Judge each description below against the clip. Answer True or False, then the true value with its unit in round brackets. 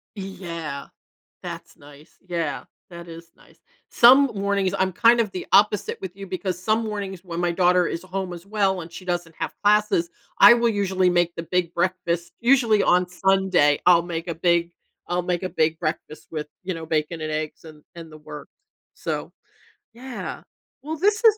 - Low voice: False (180 Hz)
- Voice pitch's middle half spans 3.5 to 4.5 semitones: False (3.0 semitones)